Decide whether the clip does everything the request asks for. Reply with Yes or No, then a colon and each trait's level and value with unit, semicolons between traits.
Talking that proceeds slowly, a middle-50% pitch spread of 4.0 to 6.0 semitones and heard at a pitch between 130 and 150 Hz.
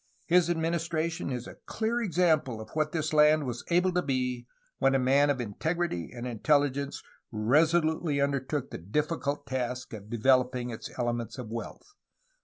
No: average, 160 wpm; average, 4.5 semitones; medium, 140 Hz